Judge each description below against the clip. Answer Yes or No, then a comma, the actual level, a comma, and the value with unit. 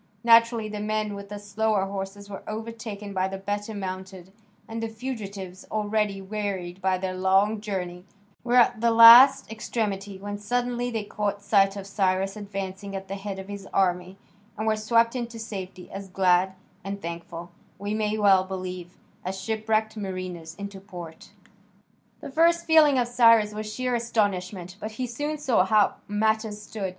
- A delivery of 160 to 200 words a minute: Yes, average, 165 wpm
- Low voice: No, high, 205 Hz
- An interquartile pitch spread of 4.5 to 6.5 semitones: No, narrow, 2.6 semitones